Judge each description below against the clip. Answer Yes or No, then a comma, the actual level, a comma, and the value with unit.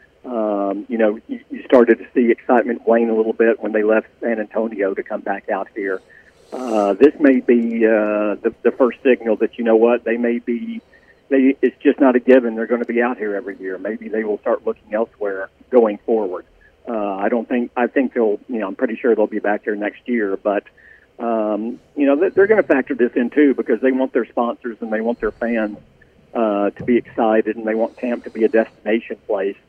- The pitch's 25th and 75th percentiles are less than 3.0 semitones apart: Yes, narrow, 2.5 semitones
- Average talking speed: No, fast, 230 wpm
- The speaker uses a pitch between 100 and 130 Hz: Yes, low, 115 Hz